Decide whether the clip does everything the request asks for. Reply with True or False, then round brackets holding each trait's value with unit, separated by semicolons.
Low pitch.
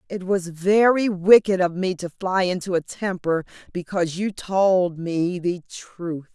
False (185 Hz)